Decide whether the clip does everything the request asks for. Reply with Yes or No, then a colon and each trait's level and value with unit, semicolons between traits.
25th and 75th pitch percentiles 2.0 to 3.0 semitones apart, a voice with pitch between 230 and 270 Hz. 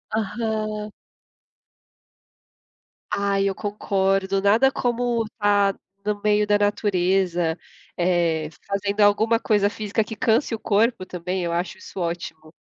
No: narrow, 2.5 semitones; high, 205 Hz